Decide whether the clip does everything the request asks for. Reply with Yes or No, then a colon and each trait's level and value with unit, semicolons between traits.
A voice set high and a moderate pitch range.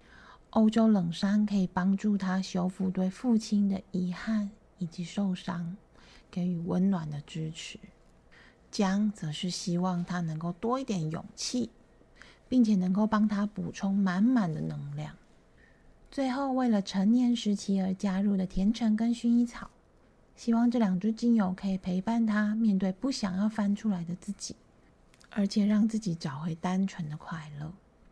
Yes: high, 195 Hz; average, 3.4 semitones